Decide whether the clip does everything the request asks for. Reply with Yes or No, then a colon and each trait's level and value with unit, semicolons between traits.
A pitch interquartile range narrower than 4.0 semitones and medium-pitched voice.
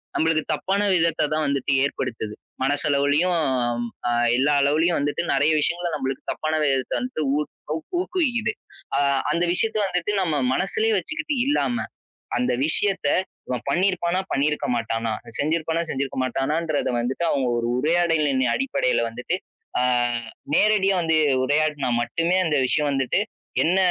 No: average, 4.5 semitones; medium, 155 Hz